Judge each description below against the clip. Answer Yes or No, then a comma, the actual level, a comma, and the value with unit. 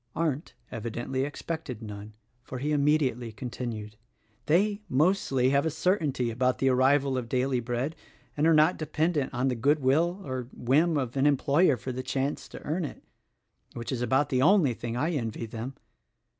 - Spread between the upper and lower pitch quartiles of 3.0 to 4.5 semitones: Yes, average, 3.7 semitones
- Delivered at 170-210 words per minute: Yes, average, 175 wpm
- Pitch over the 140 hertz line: No, low, 135 Hz